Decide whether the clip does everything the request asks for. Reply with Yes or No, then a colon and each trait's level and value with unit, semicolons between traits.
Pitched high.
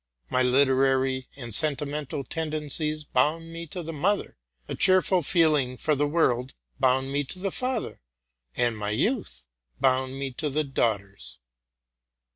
No: medium, 140 Hz